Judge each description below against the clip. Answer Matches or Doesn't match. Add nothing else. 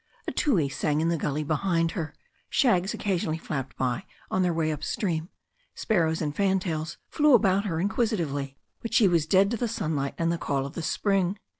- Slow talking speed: Doesn't match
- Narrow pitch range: Doesn't match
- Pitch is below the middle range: Doesn't match